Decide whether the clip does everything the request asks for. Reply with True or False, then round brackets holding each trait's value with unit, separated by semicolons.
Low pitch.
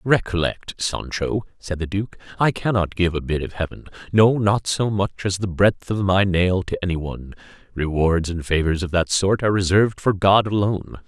True (95 Hz)